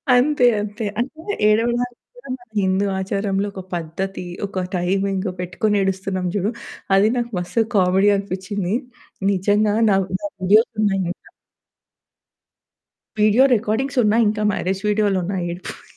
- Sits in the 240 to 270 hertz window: No, high, 200 Hz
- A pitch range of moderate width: No, narrow, 2.3 semitones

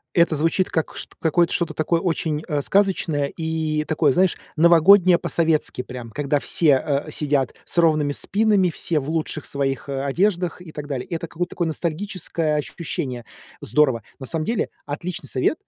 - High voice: No, medium, 160 Hz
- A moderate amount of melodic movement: Yes, average, 3.1 semitones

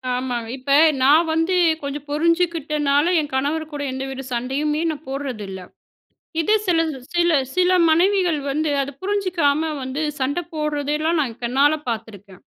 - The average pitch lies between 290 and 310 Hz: Yes, very high, 295 Hz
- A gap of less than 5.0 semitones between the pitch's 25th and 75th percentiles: Yes, average, 3.6 semitones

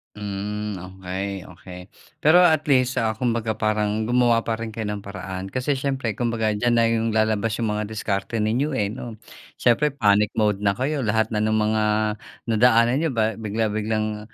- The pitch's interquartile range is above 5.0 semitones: No, narrow, 2.4 semitones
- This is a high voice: No, low, 110 Hz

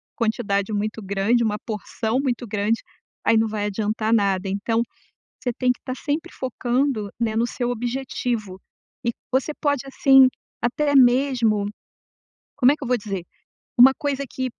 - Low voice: No, high, 235 Hz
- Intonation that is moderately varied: Yes, average, 3.5 semitones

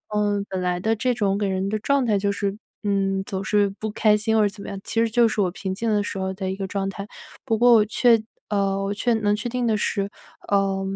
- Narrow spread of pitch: Yes, narrow, 2.2 semitones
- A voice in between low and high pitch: No, high, 205 Hz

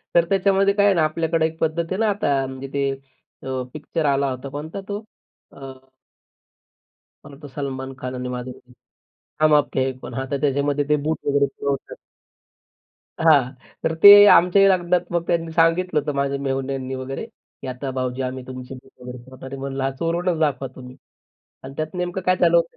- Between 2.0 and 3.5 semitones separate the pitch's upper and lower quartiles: No, average, 4.1 semitones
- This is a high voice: No, medium, 140 Hz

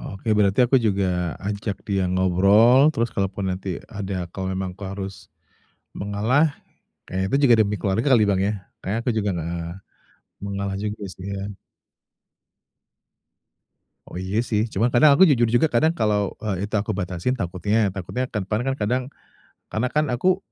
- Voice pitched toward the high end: No, low, 100 Hz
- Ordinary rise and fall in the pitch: Yes, average, 3.5 semitones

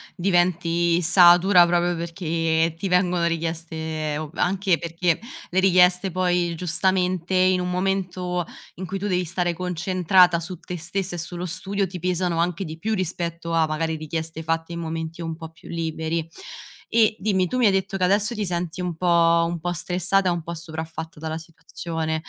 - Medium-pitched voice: Yes, medium, 175 Hz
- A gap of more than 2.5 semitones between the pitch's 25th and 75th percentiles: No, narrow, 1.9 semitones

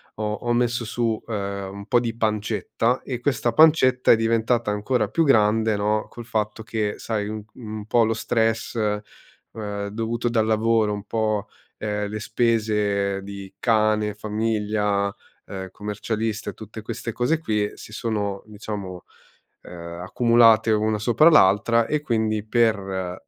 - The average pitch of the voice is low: Yes, low, 110 Hz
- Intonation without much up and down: Yes, narrow, 1.9 semitones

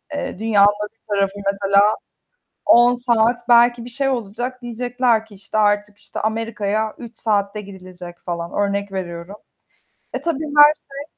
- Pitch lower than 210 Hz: No, high, 215 Hz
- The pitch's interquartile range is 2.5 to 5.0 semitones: Yes, average, 3.3 semitones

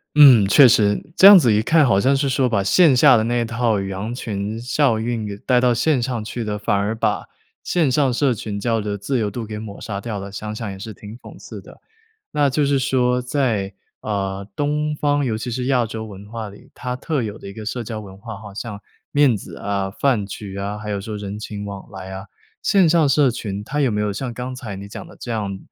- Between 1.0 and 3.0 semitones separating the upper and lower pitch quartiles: No, average, 4.0 semitones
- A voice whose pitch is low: Yes, low, 110 Hz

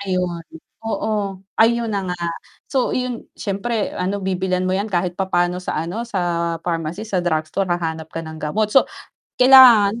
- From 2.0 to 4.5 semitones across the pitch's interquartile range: Yes, average, 3.9 semitones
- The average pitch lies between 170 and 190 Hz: Yes, medium, 185 Hz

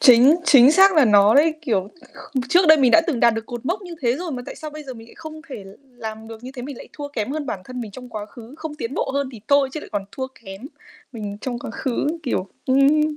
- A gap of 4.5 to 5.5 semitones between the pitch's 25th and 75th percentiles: Yes, average, 4.8 semitones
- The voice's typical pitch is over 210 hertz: Yes, very high, 260 Hz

